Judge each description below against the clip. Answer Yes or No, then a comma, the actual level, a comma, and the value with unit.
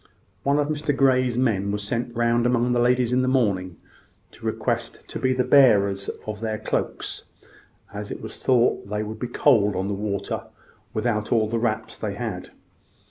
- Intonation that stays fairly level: No, average, 3.3 semitones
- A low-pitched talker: Yes, low, 115 Hz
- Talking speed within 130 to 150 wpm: No, average, 185 wpm